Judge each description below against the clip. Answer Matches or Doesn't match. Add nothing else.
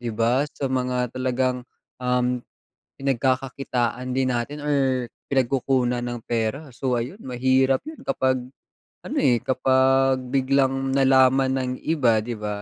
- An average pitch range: Doesn't match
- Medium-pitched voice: Doesn't match